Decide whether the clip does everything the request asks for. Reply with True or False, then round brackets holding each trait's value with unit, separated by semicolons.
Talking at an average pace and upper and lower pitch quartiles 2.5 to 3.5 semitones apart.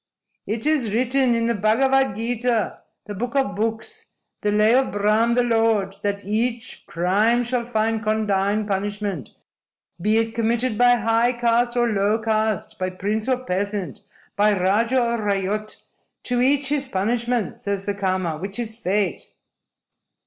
True (150 wpm; 2.9 semitones)